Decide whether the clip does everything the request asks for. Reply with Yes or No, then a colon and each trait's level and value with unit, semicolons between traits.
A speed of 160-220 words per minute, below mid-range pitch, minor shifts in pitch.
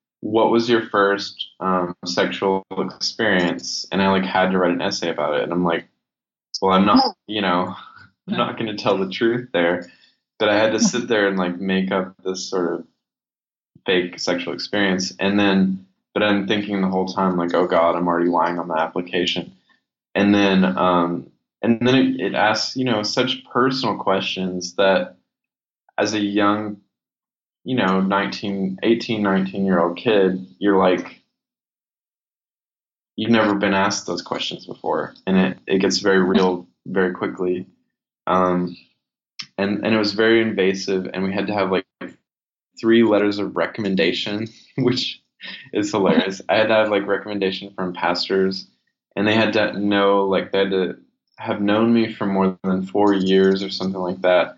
Yes: average, 175 wpm; very low, 95 Hz; narrow, 2.1 semitones